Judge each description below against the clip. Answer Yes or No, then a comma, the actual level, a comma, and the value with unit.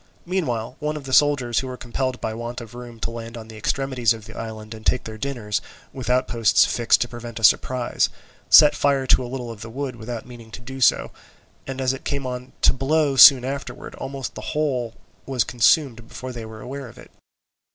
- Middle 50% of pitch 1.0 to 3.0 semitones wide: Yes, average, 2.7 semitones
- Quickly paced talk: Yes, fast, 215 wpm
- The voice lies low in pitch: Yes, low, 125 Hz